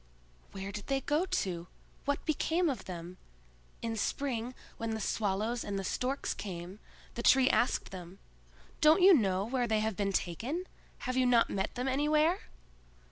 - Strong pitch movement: Yes, wide, 5.8 semitones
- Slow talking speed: No, average, 165 wpm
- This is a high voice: Yes, high, 230 Hz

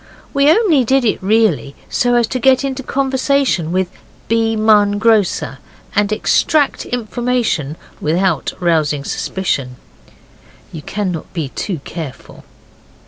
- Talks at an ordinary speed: No, slow, 120 wpm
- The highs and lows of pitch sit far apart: Yes, wide, 6.7 semitones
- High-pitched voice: Yes, high, 215 Hz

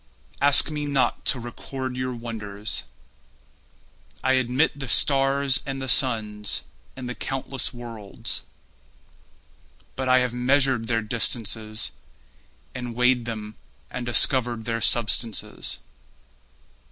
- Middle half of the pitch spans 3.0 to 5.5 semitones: No, narrow, 2.6 semitones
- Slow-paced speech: Yes, slow, 110 wpm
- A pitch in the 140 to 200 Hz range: No, low, 125 Hz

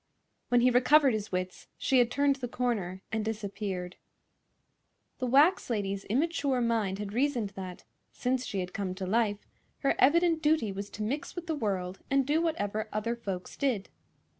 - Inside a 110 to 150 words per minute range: No, average, 170 wpm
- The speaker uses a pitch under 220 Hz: No, high, 230 Hz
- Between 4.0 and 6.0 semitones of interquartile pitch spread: Yes, wide, 5.5 semitones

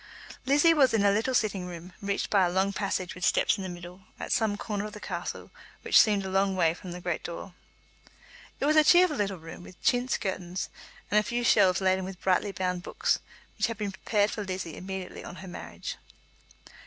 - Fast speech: Yes, fast, 215 wpm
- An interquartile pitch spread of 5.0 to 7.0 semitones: No, average, 2.7 semitones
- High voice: Yes, high, 195 Hz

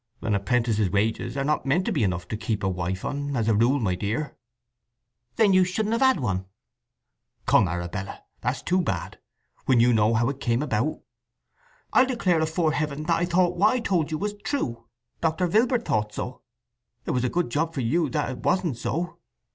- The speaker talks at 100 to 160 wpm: No, average, 200 wpm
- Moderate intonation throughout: No, wide, 8.0 semitones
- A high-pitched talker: No, medium, 140 Hz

